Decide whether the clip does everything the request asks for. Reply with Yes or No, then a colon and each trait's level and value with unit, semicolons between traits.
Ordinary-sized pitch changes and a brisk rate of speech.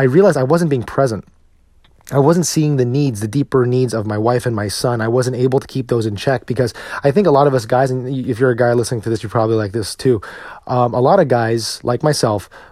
Yes: average, 3.2 semitones; fast, 265 wpm